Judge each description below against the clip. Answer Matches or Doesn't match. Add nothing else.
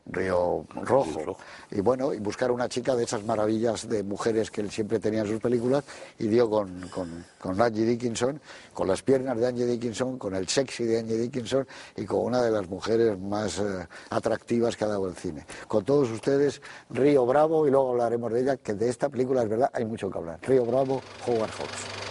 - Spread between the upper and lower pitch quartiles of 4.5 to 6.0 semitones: Doesn't match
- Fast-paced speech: Matches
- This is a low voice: Matches